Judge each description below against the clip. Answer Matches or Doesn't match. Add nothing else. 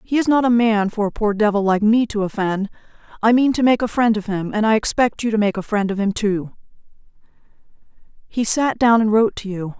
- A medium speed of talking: Doesn't match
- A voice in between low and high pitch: Doesn't match